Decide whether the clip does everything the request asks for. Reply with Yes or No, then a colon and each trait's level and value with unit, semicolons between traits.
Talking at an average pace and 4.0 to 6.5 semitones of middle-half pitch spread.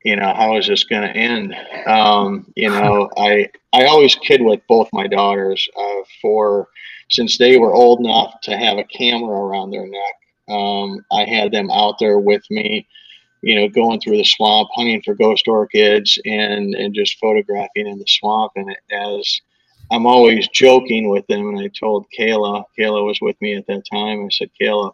No: average, 190 wpm; narrow, 2.4 semitones